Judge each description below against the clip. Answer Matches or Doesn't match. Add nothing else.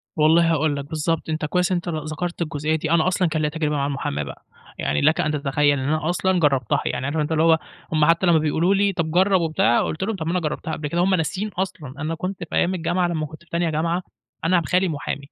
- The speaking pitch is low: Doesn't match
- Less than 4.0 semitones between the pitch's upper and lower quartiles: Matches